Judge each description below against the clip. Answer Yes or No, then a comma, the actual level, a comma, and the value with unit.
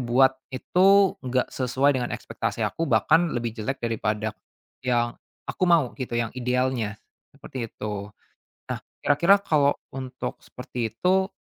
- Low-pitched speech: Yes, low, 130 Hz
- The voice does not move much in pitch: No, average, 3.6 semitones